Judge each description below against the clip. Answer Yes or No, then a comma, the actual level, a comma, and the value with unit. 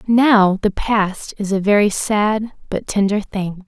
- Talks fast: No, average, 165 wpm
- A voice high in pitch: Yes, high, 205 Hz